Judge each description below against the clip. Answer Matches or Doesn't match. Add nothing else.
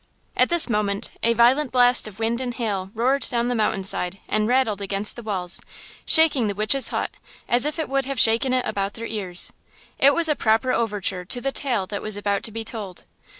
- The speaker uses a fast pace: Matches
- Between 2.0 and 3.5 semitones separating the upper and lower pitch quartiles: Doesn't match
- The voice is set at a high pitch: Matches